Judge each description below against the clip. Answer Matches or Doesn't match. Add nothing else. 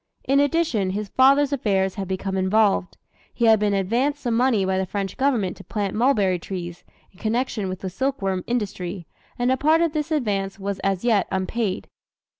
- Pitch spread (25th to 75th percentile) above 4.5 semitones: Matches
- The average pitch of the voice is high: Matches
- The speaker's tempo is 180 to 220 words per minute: Matches